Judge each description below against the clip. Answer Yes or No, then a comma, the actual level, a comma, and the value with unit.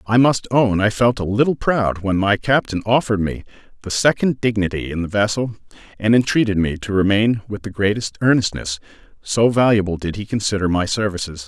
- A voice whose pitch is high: No, low, 105 Hz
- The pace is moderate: Yes, average, 185 wpm